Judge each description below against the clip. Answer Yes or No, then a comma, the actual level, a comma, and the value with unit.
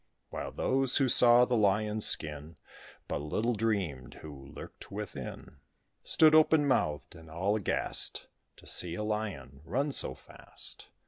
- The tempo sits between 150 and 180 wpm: No, average, 140 wpm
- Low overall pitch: Yes, low, 105 Hz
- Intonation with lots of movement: Yes, wide, 7.6 semitones